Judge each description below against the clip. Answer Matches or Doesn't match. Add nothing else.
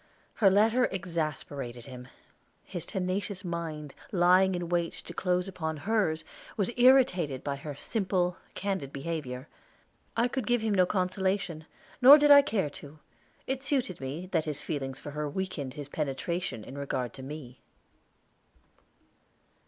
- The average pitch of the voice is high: Doesn't match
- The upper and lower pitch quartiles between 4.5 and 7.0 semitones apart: Matches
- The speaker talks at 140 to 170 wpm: Matches